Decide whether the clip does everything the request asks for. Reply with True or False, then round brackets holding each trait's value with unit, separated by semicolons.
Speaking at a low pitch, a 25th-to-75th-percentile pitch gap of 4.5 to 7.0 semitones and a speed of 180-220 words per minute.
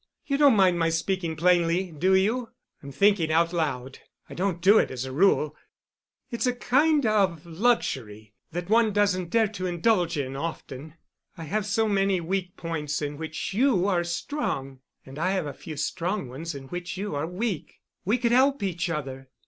False (175 Hz; 4.9 semitones; 185 wpm)